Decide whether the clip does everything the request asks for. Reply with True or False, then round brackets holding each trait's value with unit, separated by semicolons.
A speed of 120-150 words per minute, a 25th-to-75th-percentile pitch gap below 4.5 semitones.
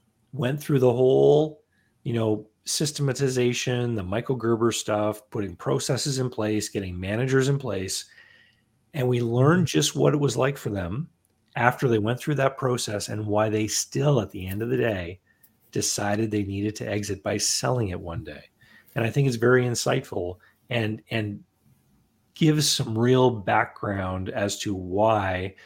False (165 wpm; 3.9 semitones)